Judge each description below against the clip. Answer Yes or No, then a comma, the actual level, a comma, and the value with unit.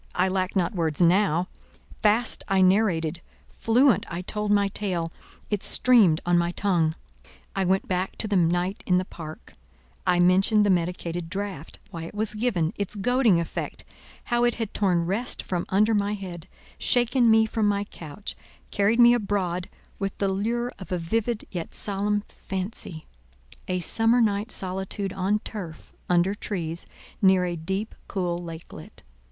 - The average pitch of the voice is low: No, high, 190 Hz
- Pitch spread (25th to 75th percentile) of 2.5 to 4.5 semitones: Yes, average, 3.3 semitones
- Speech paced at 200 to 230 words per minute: No, average, 150 wpm